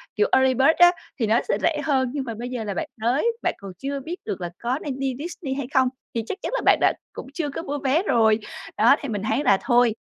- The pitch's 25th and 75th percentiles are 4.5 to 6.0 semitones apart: No, average, 4.0 semitones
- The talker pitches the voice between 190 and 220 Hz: No, very high, 265 Hz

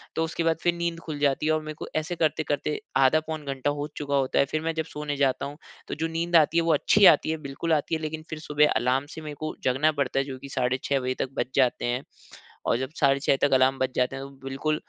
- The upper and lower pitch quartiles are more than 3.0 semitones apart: No, average, 2.7 semitones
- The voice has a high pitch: No, medium, 145 Hz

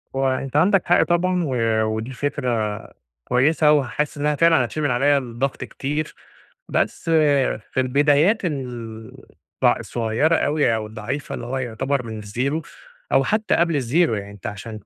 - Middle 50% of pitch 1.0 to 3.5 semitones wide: No, average, 4.8 semitones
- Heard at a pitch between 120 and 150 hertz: Yes, low, 135 Hz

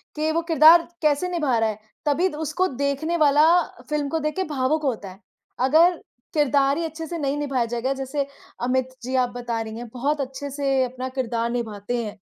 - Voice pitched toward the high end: Yes, very high, 275 Hz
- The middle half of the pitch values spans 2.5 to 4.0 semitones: Yes, average, 3.7 semitones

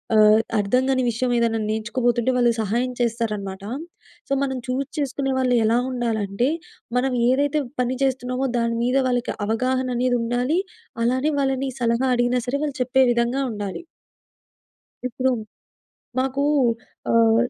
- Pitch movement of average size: No, narrow, 2.1 semitones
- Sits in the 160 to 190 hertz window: No, high, 245 Hz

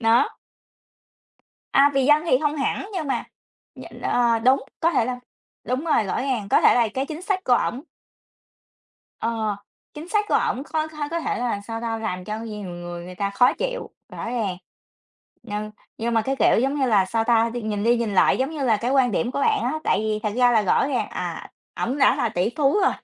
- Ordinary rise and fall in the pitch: Yes, average, 4.4 semitones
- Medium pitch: No, high, 240 Hz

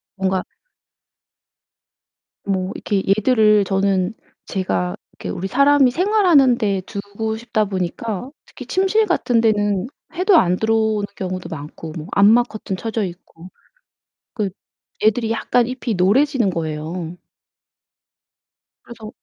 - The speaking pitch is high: Yes, high, 210 Hz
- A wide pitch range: No, average, 4.3 semitones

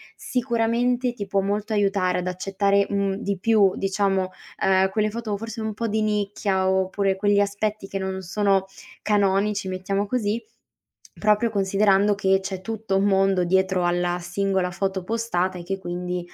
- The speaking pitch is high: Yes, high, 195 Hz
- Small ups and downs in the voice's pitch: Yes, narrow, 1.8 semitones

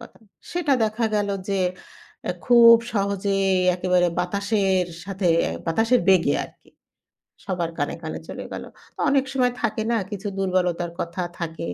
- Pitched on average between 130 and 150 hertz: No, high, 195 Hz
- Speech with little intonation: No, average, 3.7 semitones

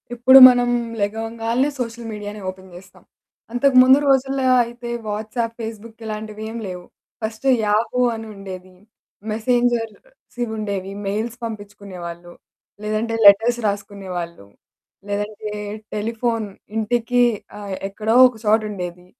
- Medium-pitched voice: No, high, 220 Hz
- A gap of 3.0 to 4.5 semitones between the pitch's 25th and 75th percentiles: No, narrow, 2.5 semitones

